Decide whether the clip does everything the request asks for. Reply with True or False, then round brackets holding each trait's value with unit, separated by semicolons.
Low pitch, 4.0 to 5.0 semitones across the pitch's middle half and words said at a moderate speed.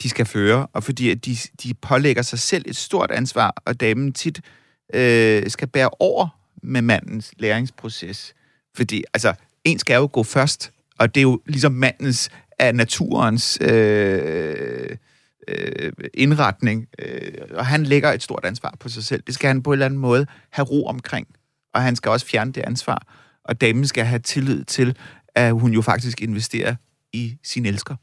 False (125 Hz; 3.2 semitones; 180 wpm)